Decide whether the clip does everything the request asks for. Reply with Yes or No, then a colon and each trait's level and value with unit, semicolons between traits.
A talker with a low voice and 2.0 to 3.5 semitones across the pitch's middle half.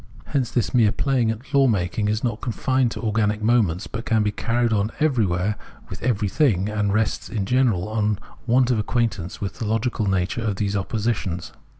Yes: low, 110 Hz; average, 2.9 semitones